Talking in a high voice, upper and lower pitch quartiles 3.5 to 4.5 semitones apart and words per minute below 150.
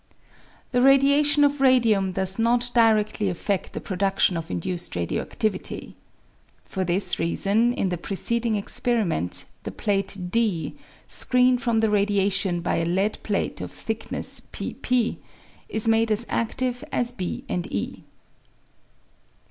Yes: high, 215 Hz; average, 4.1 semitones; average, 140 wpm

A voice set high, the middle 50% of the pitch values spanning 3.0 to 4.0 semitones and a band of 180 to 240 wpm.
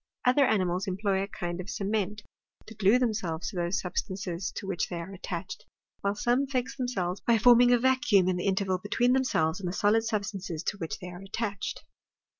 Yes: high, 200 Hz; average, 3.7 semitones; average, 200 wpm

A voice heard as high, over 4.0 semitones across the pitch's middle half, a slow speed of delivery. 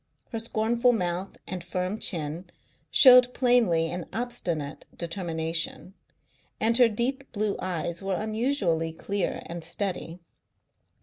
Yes: high, 195 Hz; average, 5.3 semitones; slow, 115 wpm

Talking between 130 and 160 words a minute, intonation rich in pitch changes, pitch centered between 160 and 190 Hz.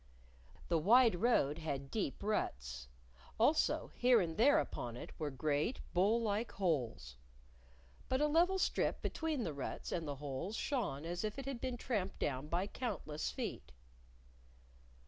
Yes: average, 150 wpm; wide, 8.8 semitones; medium, 185 Hz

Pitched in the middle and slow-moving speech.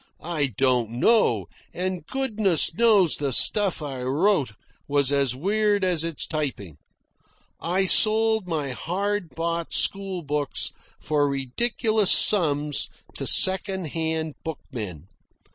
Yes: medium, 165 Hz; slow, 115 wpm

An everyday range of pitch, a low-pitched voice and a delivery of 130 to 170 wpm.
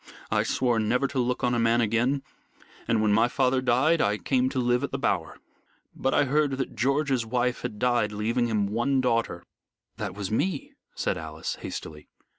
No: average, 3.4 semitones; low, 120 Hz; average, 195 wpm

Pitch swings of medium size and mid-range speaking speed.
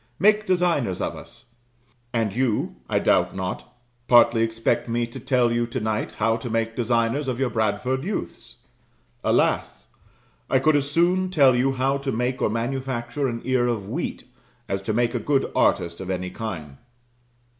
Yes: average, 3.0 semitones; average, 170 wpm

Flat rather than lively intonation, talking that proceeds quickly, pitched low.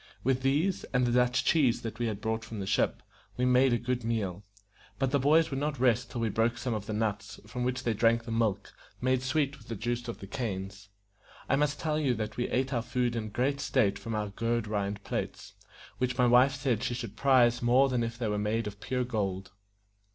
No: average, 3.0 semitones; fast, 230 wpm; low, 120 Hz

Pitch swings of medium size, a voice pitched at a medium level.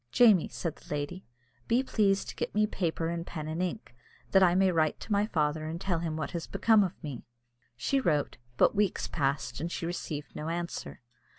Yes: average, 3.9 semitones; medium, 170 Hz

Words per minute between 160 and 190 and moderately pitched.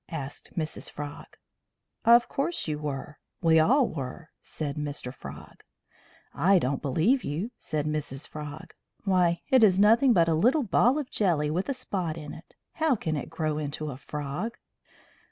Yes: average, 165 wpm; medium, 160 Hz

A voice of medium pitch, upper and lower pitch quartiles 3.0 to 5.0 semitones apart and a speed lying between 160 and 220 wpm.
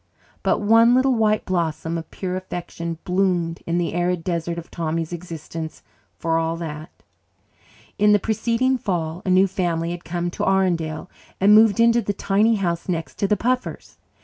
Yes: medium, 180 Hz; average, 3.7 semitones; average, 170 wpm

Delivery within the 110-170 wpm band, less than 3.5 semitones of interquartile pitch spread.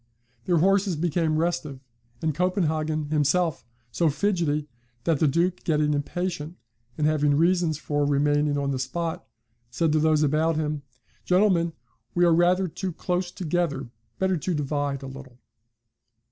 Yes: average, 145 wpm; average, 3.0 semitones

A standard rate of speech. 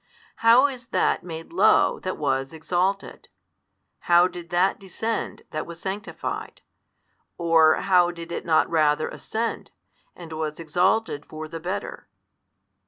No: slow, 130 wpm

